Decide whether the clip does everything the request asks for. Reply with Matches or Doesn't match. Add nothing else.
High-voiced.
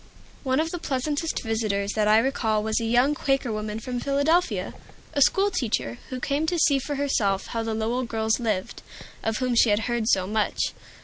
Matches